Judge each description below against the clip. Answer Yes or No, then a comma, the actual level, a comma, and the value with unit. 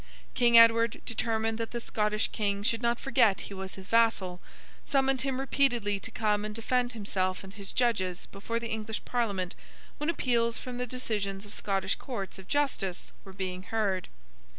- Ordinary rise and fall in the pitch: Yes, average, 3.3 semitones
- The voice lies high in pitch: Yes, high, 220 Hz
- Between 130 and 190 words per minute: Yes, average, 175 wpm